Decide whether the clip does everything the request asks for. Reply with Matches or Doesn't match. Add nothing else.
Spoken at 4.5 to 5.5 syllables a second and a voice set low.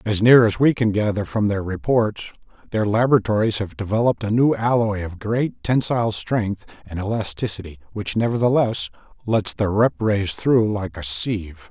Matches